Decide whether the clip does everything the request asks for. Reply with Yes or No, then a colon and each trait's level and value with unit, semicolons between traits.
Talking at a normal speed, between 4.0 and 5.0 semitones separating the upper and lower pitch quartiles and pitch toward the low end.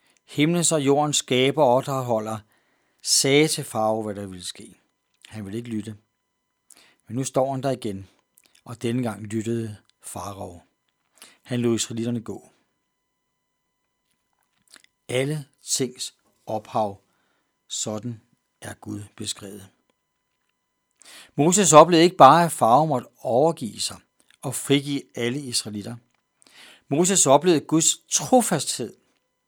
No: slow, 115 wpm; average, 4.6 semitones; low, 120 Hz